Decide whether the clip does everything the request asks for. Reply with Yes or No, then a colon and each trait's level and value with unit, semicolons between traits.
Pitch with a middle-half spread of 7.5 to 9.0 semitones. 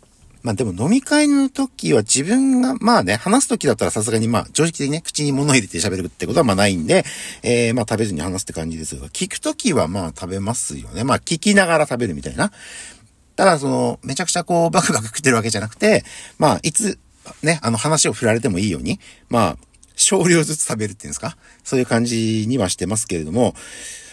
Yes: wide, 8.4 semitones